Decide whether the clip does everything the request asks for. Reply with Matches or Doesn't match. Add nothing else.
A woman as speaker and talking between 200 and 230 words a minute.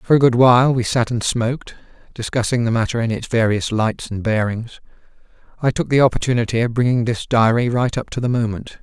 Doesn't match